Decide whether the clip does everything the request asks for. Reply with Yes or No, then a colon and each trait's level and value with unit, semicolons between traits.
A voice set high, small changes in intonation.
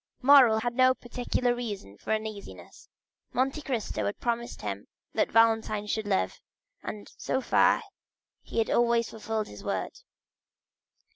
Yes: high, 230 Hz; narrow, 2.3 semitones